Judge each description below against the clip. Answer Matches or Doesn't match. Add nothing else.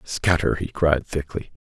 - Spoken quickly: Doesn't match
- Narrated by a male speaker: Matches